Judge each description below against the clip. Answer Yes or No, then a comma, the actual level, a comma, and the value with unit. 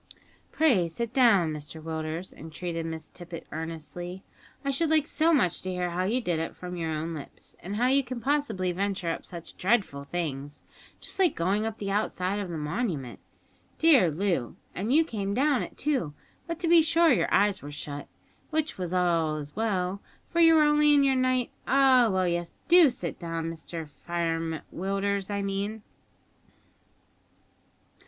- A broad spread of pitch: Yes, wide, 7.3 semitones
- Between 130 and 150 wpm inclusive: No, average, 175 wpm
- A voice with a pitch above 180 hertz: Yes, high, 190 Hz